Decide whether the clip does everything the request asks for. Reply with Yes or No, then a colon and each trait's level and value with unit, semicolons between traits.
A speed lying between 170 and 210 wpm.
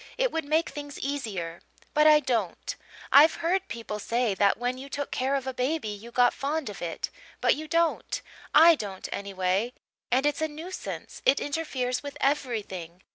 Yes: average, 180 wpm